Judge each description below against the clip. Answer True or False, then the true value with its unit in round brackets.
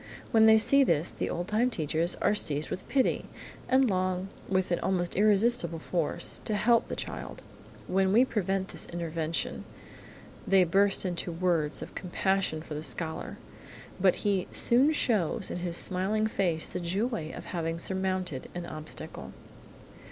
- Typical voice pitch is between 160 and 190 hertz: True (185 Hz)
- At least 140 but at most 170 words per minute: True (160 wpm)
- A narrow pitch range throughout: False (3.8 semitones)